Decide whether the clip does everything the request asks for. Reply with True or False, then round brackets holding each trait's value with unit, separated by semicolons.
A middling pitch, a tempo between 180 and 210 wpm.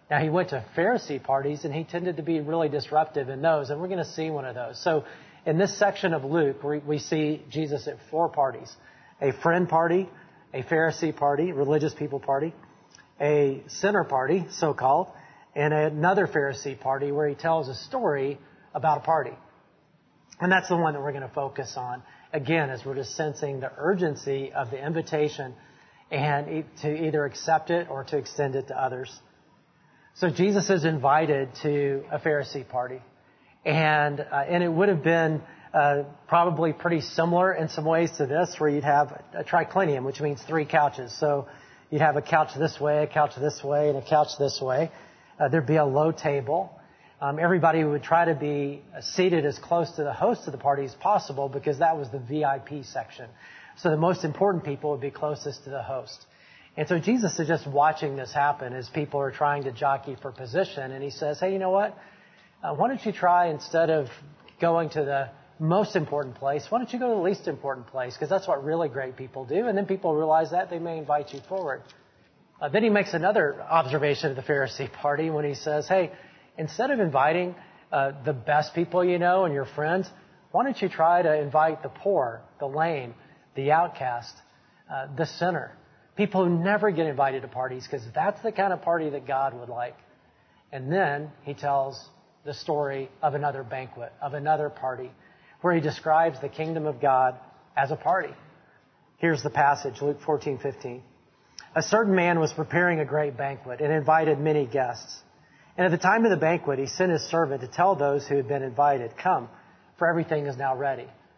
True (150 Hz; 195 wpm)